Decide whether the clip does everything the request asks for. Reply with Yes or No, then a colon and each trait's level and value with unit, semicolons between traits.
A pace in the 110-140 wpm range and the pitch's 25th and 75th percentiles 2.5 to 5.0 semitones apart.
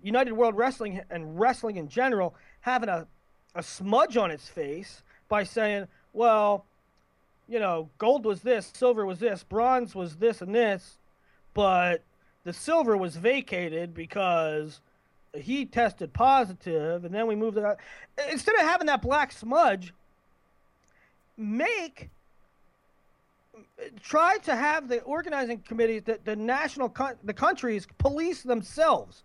No: slow, 135 wpm; wide, 5.4 semitones